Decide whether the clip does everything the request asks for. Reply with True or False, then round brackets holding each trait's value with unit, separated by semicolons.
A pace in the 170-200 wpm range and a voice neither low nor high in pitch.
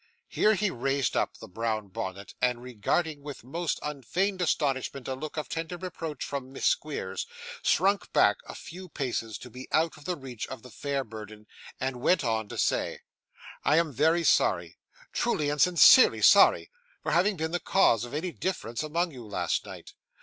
True (180 wpm; 145 Hz)